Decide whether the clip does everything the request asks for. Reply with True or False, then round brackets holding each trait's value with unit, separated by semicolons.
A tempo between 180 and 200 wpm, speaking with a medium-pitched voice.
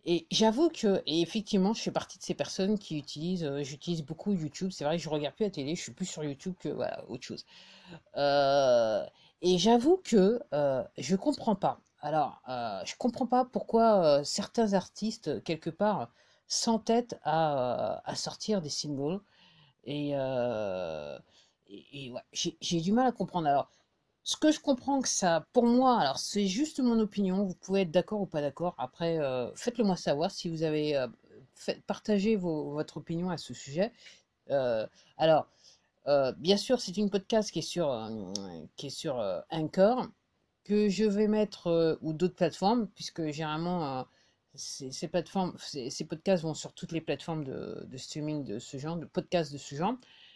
True (185 wpm; 180 Hz)